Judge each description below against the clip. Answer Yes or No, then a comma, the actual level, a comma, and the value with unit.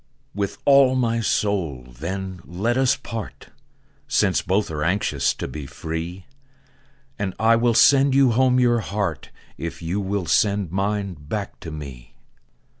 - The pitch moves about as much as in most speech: No, wide, 5.7 semitones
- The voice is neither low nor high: No, low, 100 Hz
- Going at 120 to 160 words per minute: Yes, average, 150 wpm